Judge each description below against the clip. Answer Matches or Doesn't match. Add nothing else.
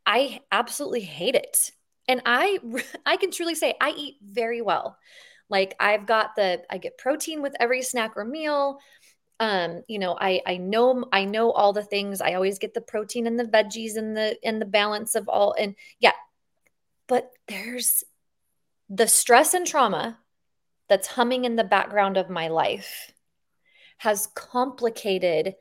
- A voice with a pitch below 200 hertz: Doesn't match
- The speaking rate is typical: Matches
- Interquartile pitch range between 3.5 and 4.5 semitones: Matches